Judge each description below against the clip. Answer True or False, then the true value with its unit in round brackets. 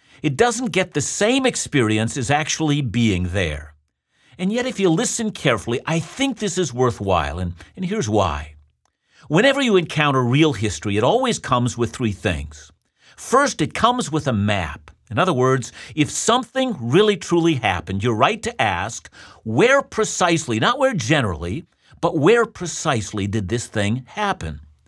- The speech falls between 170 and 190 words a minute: False (160 wpm)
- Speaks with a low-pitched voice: True (130 Hz)